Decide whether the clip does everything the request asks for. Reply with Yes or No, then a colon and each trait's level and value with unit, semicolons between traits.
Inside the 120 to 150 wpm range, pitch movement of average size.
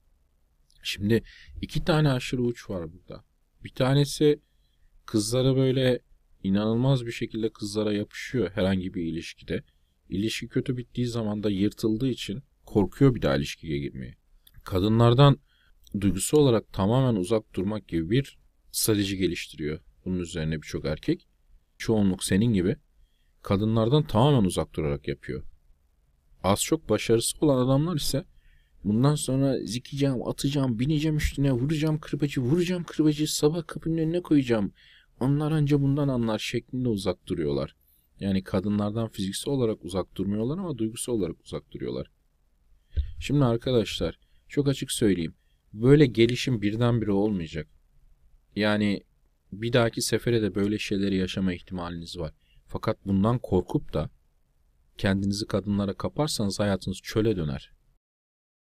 No: average, 125 wpm; wide, 7.9 semitones